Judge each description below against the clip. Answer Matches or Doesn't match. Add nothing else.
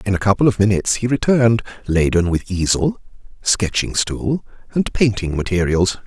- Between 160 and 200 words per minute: Doesn't match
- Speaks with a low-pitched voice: Matches